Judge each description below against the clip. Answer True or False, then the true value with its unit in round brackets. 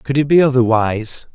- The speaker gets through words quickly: False (180 wpm)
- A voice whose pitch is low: True (125 Hz)